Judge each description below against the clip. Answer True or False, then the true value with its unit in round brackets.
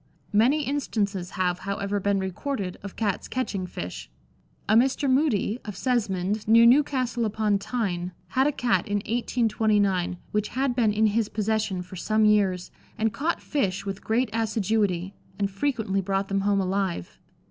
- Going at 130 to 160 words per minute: True (155 wpm)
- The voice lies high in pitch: True (210 Hz)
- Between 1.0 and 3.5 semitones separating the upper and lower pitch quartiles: True (3.2 semitones)